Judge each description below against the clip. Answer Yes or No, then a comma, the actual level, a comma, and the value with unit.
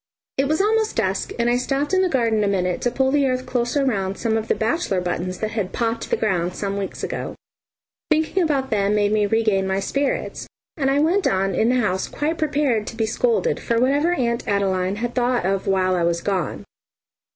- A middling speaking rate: No, fast, 215 wpm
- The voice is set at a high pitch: Yes, high, 225 Hz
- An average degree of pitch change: No, wide, 5.8 semitones